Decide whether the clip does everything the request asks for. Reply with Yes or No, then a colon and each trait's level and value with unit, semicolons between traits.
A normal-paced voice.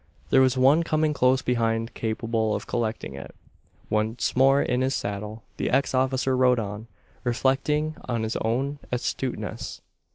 Yes: average, 150 wpm